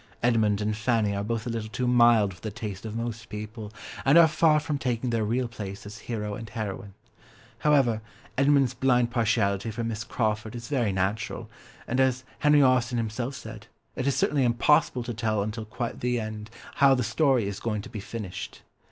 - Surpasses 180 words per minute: Yes, average, 195 wpm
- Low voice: Yes, low, 115 Hz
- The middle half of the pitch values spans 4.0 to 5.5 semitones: No, average, 2.8 semitones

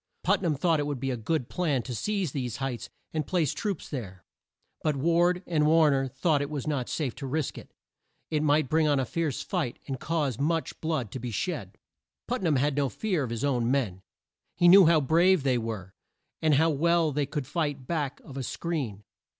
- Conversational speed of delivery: No, fast, 215 wpm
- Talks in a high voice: No, medium, 145 Hz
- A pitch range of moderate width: Yes, average, 4.0 semitones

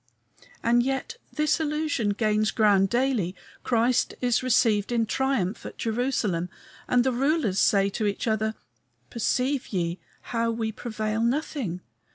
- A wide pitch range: No, average, 3.6 semitones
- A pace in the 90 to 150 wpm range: Yes, slow, 135 wpm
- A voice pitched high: Yes, high, 230 Hz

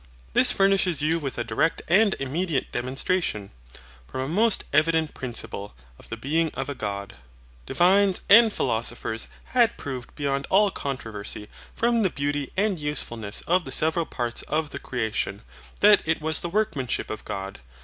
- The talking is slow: No, average, 160 wpm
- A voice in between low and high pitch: Yes, medium, 145 Hz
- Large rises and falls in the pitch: Yes, wide, 7.1 semitones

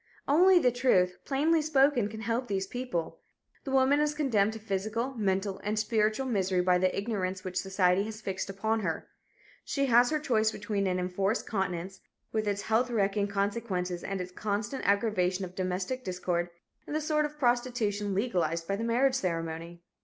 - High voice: Yes, high, 210 Hz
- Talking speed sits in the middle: Yes, average, 175 wpm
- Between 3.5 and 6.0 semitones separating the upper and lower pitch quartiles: Yes, average, 4.7 semitones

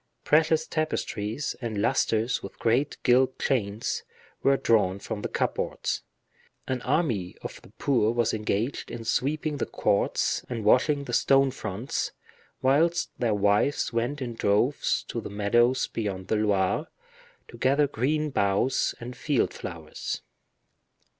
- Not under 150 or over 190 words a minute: No, slow, 135 wpm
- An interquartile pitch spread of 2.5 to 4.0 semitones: No, average, 4.7 semitones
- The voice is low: Yes, low, 120 Hz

